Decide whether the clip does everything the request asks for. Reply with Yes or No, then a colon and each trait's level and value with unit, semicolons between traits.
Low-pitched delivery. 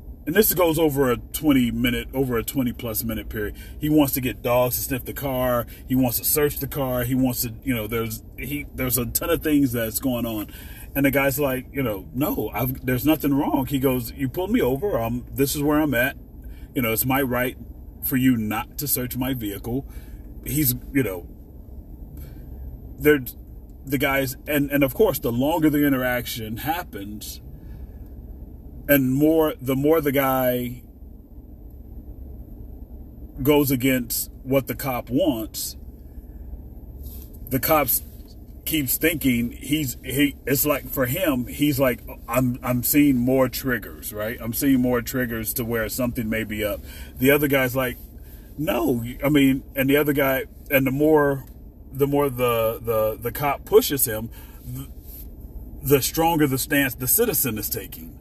Yes: low, 125 Hz